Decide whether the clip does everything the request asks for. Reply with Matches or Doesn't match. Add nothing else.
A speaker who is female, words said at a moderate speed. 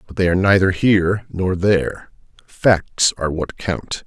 Doesn't match